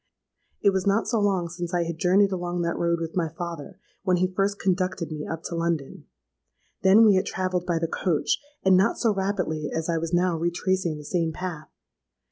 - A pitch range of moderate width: No, narrow, 2.3 semitones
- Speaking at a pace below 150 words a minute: No, average, 200 wpm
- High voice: No, medium, 175 Hz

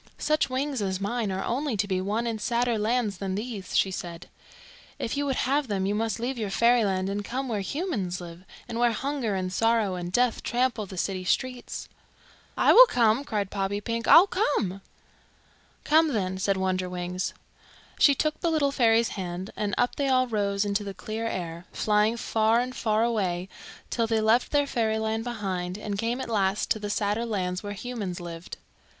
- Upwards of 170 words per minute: Yes, average, 190 wpm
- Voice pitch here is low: No, high, 215 Hz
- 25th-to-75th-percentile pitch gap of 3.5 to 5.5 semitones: Yes, average, 4.1 semitones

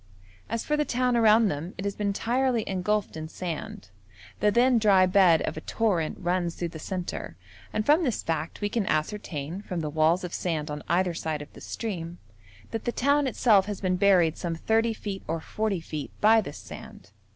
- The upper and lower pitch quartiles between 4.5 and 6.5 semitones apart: Yes, average, 5.1 semitones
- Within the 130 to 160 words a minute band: No, average, 200 wpm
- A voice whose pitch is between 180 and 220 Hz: Yes, high, 190 Hz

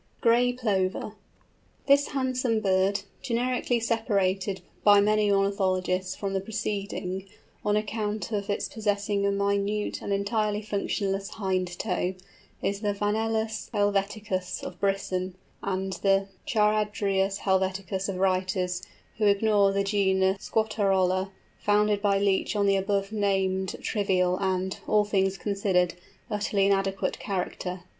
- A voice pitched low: No, high, 200 Hz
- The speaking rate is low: Yes, slow, 120 wpm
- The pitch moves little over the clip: Yes, narrow, 1.7 semitones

